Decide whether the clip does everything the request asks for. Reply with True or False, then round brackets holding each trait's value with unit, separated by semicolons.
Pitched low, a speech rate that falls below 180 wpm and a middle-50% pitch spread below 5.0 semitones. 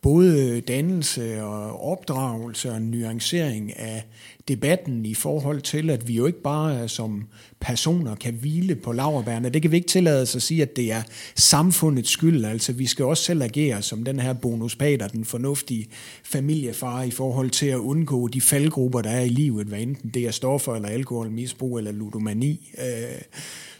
True (125 Hz; 170 wpm; 4.1 semitones)